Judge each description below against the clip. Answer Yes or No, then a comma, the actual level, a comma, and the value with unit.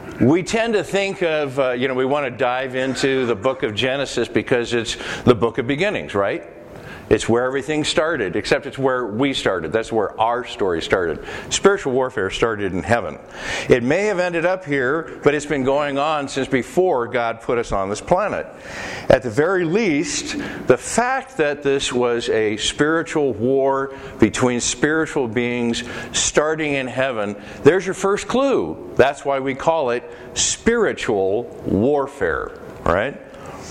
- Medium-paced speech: Yes, average, 165 wpm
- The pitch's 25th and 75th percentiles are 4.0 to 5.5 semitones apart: Yes, average, 4.4 semitones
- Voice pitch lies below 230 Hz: Yes, low, 135 Hz